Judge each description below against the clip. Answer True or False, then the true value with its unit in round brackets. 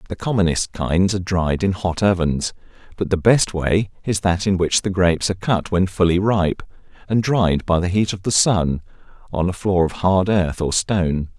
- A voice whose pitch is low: True (90 Hz)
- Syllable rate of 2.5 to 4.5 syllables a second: False (4.9 syllables/s)